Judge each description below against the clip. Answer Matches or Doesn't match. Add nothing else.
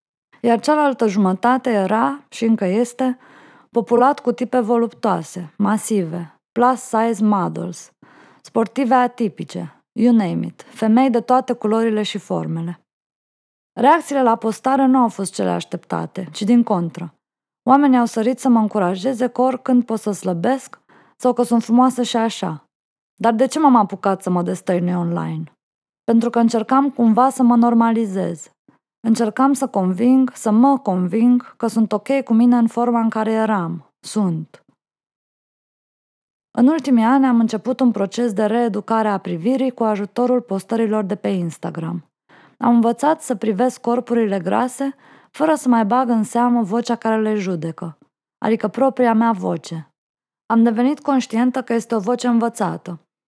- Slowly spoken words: Doesn't match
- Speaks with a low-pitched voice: Doesn't match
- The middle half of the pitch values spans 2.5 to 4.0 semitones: Matches